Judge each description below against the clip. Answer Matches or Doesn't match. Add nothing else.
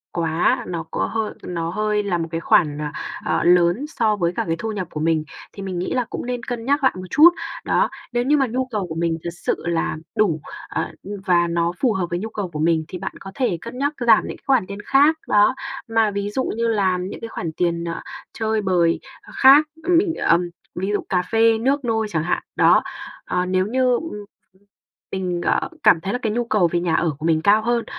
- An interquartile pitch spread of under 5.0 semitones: Doesn't match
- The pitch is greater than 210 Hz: Doesn't match